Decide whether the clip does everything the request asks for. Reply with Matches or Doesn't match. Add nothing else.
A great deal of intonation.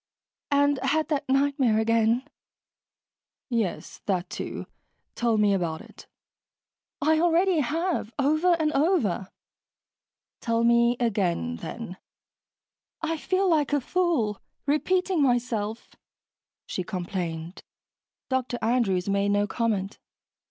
Matches